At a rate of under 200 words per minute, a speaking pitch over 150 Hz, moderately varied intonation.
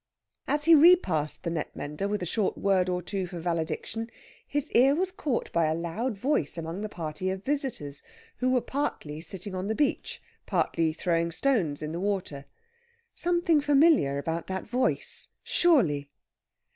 No: average, 165 wpm; high, 190 Hz; wide, 8.5 semitones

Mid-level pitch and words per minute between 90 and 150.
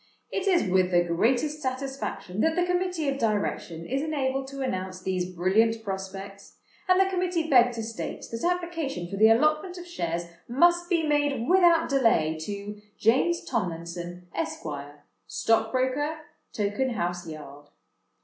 No: high, 240 Hz; average, 140 wpm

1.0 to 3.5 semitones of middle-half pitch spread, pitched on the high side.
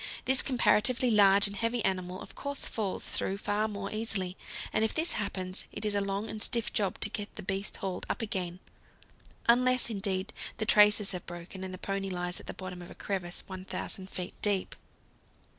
Yes: narrow, 2.6 semitones; high, 200 Hz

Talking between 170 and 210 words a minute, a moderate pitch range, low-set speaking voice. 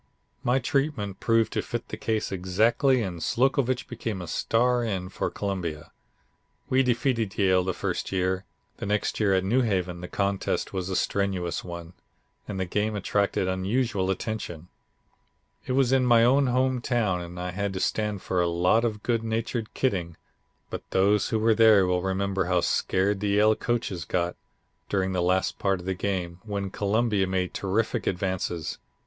Yes: average, 175 wpm; average, 3.7 semitones; low, 100 Hz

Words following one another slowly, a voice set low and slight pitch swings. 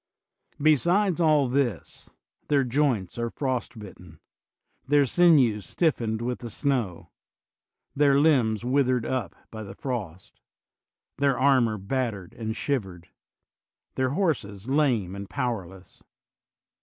No: slow, 125 wpm; low, 125 Hz; average, 4.7 semitones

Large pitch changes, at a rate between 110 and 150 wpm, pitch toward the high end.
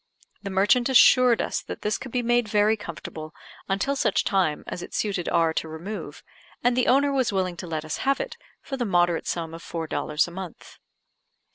No: wide, 6.4 semitones; fast, 205 wpm; high, 195 Hz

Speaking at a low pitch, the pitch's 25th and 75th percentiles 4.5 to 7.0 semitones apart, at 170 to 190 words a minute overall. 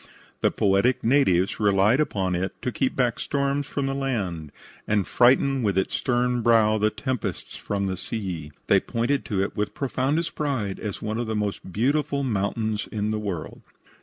Yes: low, 110 Hz; average, 4.9 semitones; average, 175 wpm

